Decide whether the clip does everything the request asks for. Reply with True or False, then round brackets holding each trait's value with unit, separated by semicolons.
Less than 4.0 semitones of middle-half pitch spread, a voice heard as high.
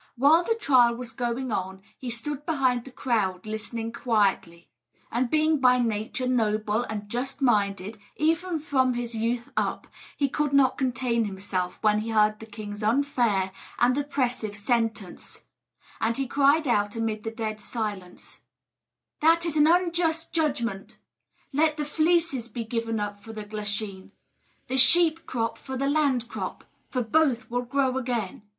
False (4.4 semitones; 240 Hz)